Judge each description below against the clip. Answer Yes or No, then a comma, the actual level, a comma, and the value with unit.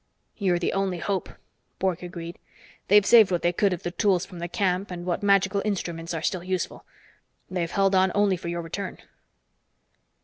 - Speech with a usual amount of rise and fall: No, narrow, 2.2 semitones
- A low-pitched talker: No, medium, 185 Hz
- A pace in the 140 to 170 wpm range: No, average, 180 wpm